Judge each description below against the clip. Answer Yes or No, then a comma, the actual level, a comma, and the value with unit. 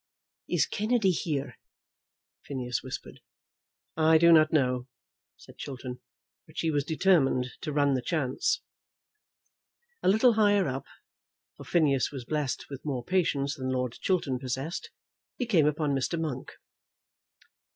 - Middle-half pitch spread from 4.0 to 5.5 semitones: Yes, average, 4.3 semitones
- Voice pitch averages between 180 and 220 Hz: No, medium, 145 Hz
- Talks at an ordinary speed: No, slow, 130 wpm